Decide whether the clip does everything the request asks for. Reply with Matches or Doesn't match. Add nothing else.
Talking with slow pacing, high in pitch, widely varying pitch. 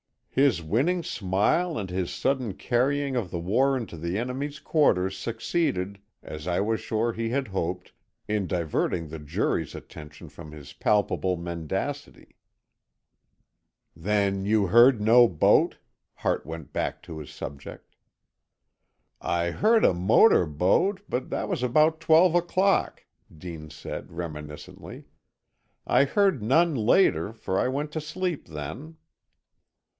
Doesn't match